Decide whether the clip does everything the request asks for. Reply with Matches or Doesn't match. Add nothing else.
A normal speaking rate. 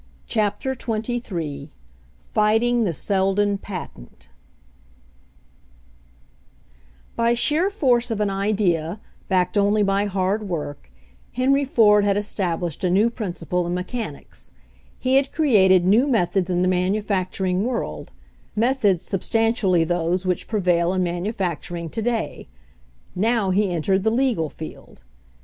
Doesn't match